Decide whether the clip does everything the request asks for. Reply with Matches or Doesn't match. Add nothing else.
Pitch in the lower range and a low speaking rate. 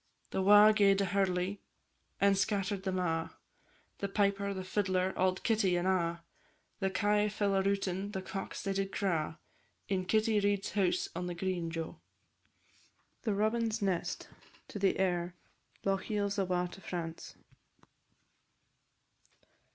Doesn't match